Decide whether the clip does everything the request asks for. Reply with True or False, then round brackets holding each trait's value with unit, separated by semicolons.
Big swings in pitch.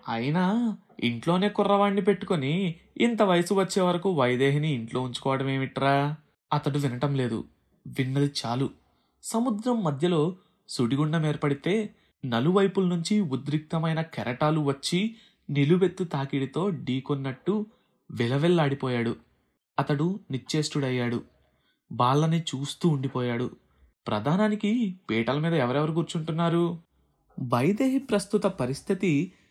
True (6.1 semitones)